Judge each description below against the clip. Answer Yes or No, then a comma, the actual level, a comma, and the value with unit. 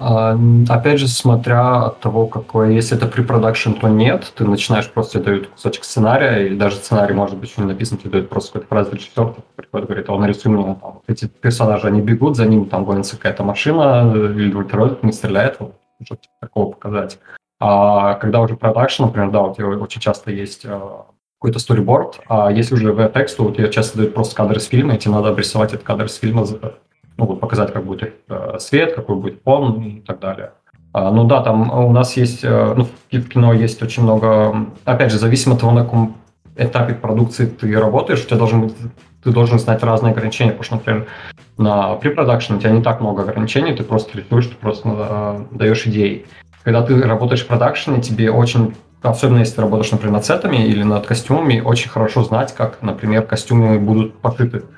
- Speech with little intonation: Yes, narrow, 2.1 semitones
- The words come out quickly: Yes, fast, 200 wpm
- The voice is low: Yes, low, 110 Hz